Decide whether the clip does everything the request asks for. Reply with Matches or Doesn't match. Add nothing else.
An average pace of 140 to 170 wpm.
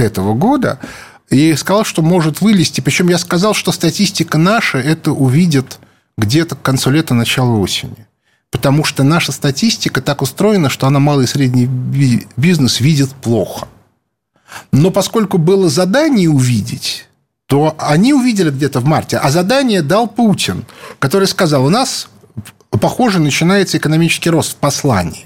Matches